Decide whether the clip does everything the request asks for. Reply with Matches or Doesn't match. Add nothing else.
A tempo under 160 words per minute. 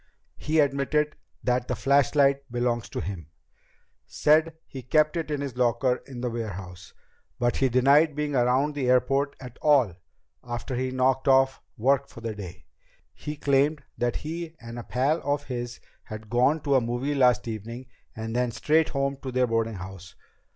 Doesn't match